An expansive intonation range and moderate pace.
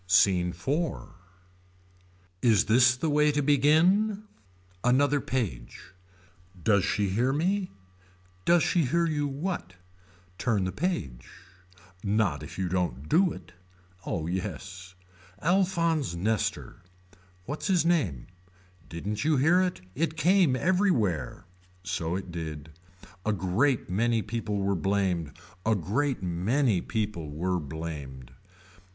No: wide, 8.9 semitones; slow, 120 wpm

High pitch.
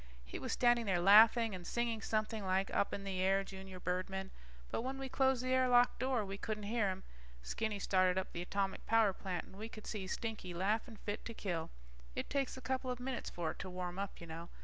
Yes: high, 200 Hz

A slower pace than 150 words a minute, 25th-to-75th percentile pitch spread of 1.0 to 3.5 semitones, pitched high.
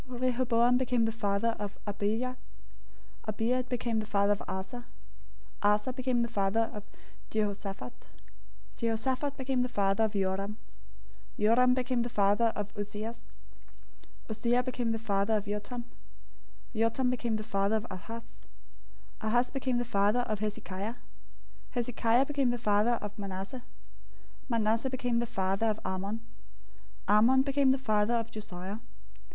Yes: average, 140 wpm; average, 3.1 semitones; high, 225 Hz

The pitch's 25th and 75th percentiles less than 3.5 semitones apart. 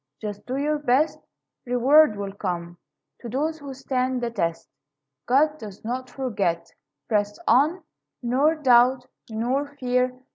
No: average, 4.6 semitones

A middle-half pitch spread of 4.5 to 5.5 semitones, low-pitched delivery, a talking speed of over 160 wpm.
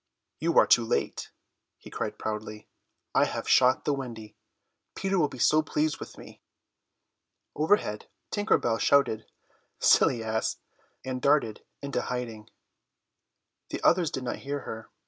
No: average, 4.9 semitones; low, 125 Hz; average, 140 wpm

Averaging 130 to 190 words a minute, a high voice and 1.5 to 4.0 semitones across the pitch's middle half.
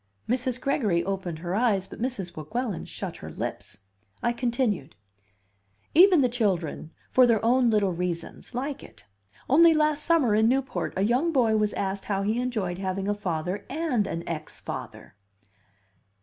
No: average, 160 wpm; high, 220 Hz; average, 5.2 semitones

